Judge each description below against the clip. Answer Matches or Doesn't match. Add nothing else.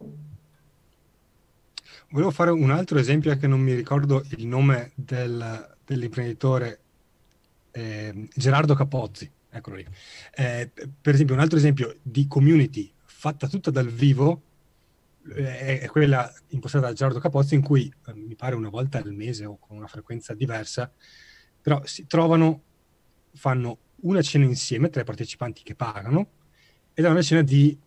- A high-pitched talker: Doesn't match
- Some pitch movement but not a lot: Matches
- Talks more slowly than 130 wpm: Doesn't match